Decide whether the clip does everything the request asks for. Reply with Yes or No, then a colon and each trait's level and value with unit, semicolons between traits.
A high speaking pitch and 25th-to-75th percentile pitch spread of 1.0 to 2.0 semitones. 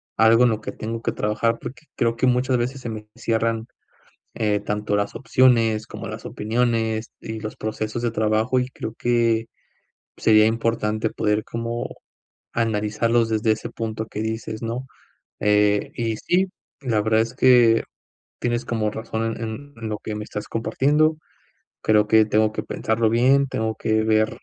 No: low, 110 Hz; narrow, 1.5 semitones